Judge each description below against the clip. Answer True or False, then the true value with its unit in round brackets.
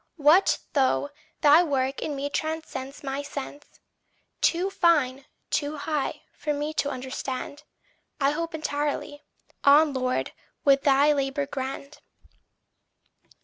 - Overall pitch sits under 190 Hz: False (285 Hz)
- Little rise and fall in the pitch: True (1.9 semitones)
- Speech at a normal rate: False (115 wpm)